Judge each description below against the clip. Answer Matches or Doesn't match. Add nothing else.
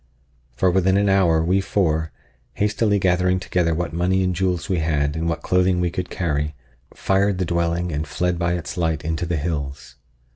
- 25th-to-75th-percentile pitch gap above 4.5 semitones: Doesn't match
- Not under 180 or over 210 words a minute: Matches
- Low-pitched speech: Matches